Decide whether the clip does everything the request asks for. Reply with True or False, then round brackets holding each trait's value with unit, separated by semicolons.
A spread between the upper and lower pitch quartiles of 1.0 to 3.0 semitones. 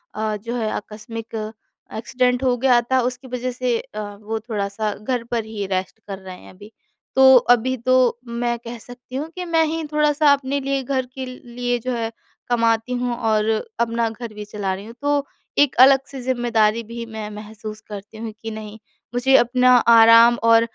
True (2.7 semitones)